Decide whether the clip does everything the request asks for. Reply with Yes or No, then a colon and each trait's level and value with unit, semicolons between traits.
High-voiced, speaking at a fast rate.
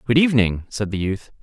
No: low, 115 Hz; fast, 210 wpm